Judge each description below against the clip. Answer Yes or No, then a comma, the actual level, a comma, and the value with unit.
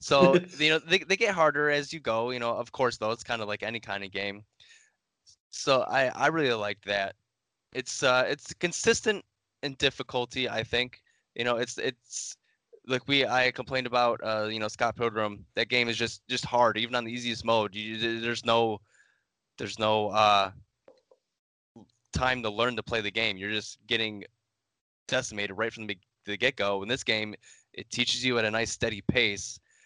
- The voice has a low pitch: Yes, low, 115 Hz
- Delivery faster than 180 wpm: Yes, average, 195 wpm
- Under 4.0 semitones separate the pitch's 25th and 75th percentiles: Yes, average, 3.0 semitones